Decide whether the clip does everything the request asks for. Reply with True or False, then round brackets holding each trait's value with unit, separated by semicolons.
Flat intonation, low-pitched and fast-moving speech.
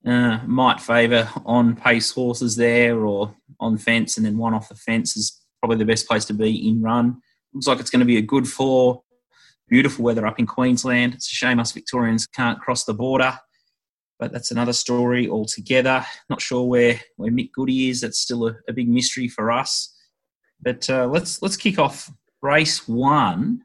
False (2.0 semitones; 120 Hz; 195 wpm)